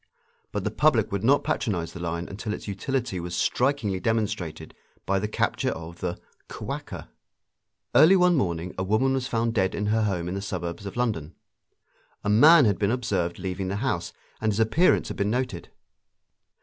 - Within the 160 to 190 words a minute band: Yes, average, 180 wpm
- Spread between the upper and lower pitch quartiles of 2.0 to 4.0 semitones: No, average, 5.0 semitones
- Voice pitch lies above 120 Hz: No, low, 100 Hz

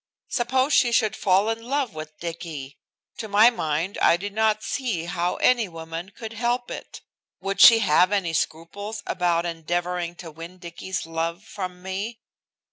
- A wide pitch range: No, average, 4.7 semitones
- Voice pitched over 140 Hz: Yes, medium, 185 Hz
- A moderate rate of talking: Yes, average, 160 wpm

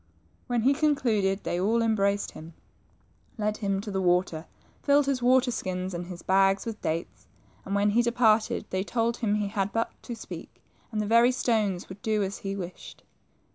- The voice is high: Yes, high, 210 Hz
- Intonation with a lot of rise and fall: No, average, 3.4 semitones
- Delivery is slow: No, average, 185 wpm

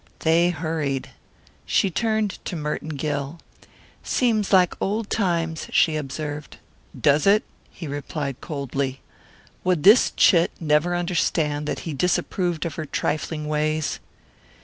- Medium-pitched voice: Yes, medium, 160 Hz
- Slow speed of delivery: Yes, slow, 125 wpm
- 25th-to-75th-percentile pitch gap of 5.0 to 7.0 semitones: No, average, 3.2 semitones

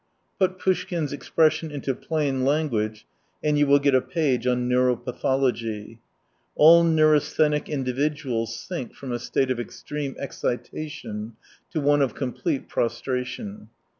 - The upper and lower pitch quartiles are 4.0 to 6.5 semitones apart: No, average, 3.6 semitones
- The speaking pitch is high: No, low, 135 Hz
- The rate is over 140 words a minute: No, slow, 135 wpm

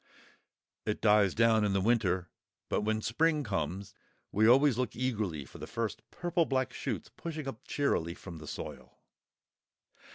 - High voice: No, low, 110 Hz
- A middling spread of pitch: Yes, average, 5.0 semitones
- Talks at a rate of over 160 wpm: No, average, 155 wpm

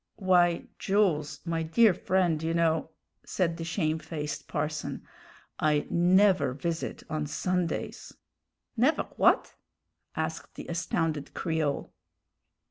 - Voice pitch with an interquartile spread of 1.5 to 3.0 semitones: Yes, average, 2.7 semitones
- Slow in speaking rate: Yes, slow, 105 wpm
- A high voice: No, medium, 165 Hz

